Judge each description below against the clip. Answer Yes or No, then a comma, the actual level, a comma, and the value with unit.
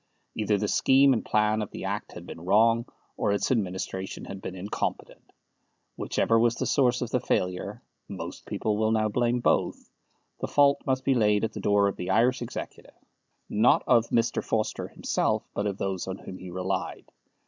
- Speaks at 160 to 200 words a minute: Yes, average, 185 wpm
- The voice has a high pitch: No, low, 110 Hz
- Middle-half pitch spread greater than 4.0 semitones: No, average, 3.4 semitones